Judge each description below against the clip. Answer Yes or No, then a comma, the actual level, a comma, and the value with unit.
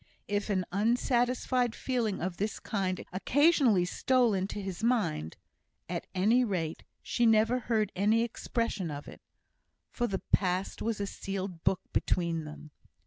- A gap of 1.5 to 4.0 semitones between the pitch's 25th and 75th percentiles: No, average, 4.4 semitones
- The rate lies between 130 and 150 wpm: Yes, average, 140 wpm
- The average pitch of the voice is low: No, high, 205 Hz